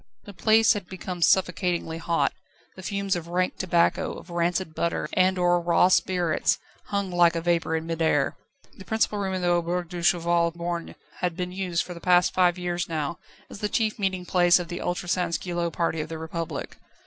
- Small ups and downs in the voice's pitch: Yes, narrow, 1.5 semitones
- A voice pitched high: No, medium, 175 Hz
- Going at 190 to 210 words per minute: Yes, average, 195 wpm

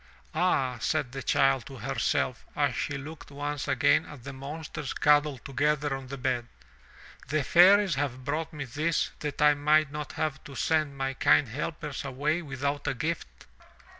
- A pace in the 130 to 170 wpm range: Yes, average, 165 wpm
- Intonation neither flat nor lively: No, narrow, 2.1 semitones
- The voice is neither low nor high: Yes, medium, 145 Hz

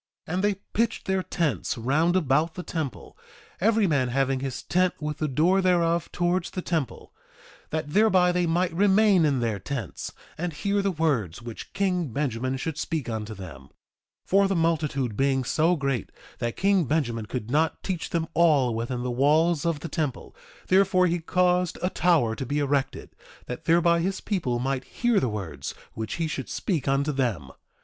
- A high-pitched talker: No, medium, 155 Hz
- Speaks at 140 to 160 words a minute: No, average, 180 wpm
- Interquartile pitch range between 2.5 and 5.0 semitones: No, wide, 5.6 semitones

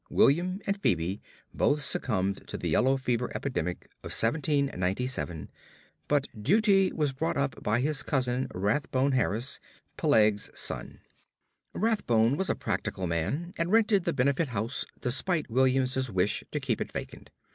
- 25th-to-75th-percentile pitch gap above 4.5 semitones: Yes, wide, 5.4 semitones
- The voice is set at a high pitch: No, low, 130 Hz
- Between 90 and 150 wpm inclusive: Yes, average, 145 wpm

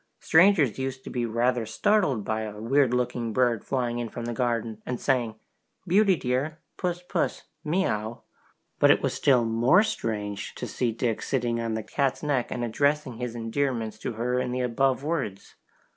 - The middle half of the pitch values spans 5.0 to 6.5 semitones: No, average, 3.4 semitones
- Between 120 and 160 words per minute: No, average, 175 wpm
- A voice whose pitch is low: Yes, low, 125 Hz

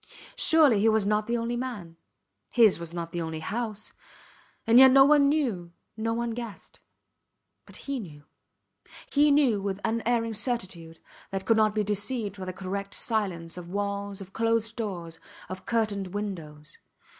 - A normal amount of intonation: Yes, average, 3.9 semitones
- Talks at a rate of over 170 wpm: No, average, 160 wpm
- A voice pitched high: Yes, high, 210 Hz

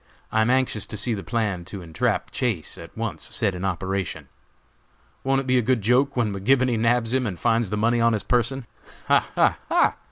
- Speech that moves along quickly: Yes, fast, 210 wpm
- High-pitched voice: No, low, 115 Hz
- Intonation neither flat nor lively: Yes, average, 4.0 semitones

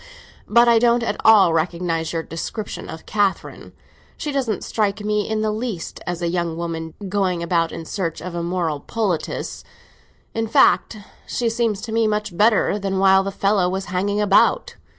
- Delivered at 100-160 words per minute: No, average, 175 wpm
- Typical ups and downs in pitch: Yes, average, 4.1 semitones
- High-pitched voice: Yes, high, 195 Hz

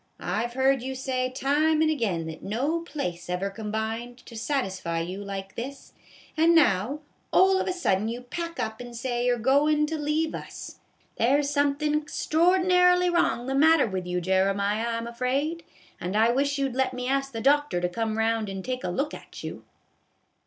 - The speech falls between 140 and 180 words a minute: No, average, 195 wpm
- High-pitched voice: Yes, very high, 255 Hz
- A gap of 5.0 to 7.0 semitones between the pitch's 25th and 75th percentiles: Yes, average, 5.3 semitones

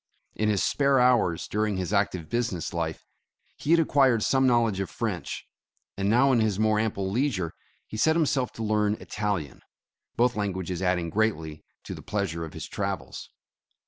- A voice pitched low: Yes, low, 105 Hz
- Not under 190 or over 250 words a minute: No, average, 175 wpm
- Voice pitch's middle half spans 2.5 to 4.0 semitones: No, average, 4.5 semitones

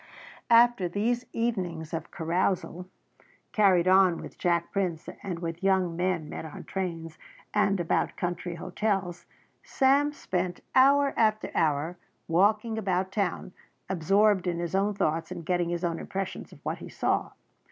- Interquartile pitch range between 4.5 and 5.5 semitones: No, average, 3.2 semitones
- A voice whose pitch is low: No, medium, 185 Hz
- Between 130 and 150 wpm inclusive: Yes, average, 145 wpm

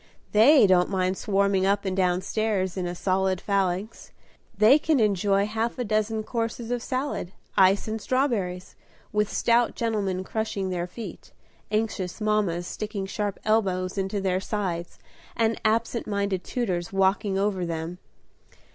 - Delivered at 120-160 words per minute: Yes, average, 145 wpm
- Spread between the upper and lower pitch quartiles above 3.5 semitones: No, average, 2.9 semitones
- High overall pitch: Yes, high, 200 Hz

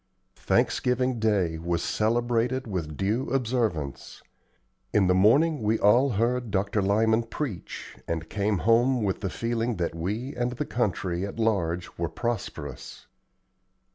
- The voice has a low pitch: Yes, low, 110 Hz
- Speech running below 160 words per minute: Yes, slow, 135 wpm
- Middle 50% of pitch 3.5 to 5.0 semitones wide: Yes, average, 4.7 semitones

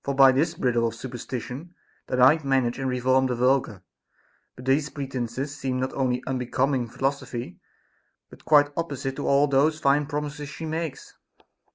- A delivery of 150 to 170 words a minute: Yes, average, 155 wpm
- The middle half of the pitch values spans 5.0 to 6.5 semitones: No, narrow, 2.4 semitones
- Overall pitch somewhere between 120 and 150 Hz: Yes, low, 135 Hz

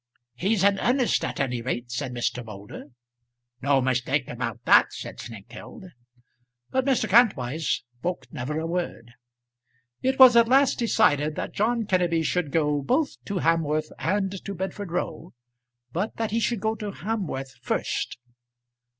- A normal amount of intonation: No, wide, 8.2 semitones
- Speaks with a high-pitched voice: No, medium, 175 Hz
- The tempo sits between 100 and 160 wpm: Yes, average, 150 wpm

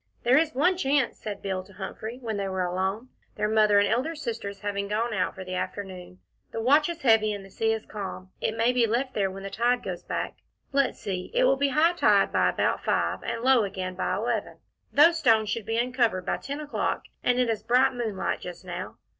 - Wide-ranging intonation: No, average, 4.5 semitones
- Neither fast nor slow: No, fast, 225 wpm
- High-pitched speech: Yes, high, 225 Hz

